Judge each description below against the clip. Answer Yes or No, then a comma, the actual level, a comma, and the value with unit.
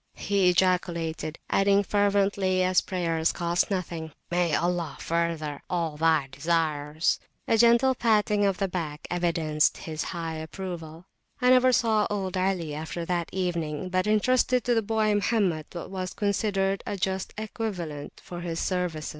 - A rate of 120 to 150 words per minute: Yes, average, 145 wpm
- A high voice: No, medium, 180 Hz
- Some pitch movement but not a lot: Yes, average, 3.6 semitones